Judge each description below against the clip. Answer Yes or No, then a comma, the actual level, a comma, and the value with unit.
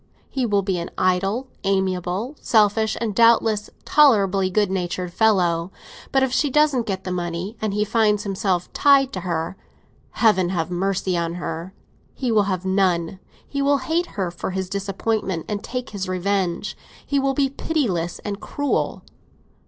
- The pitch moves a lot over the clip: No, average, 4.0 semitones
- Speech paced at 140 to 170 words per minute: Yes, average, 160 wpm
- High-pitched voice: Yes, high, 195 Hz